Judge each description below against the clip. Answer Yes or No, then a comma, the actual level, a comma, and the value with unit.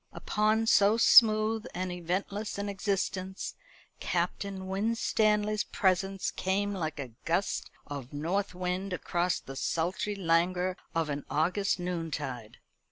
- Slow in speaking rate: Yes, slow, 115 wpm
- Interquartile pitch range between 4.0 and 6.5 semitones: No, average, 3.0 semitones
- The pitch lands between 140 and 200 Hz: Yes, high, 190 Hz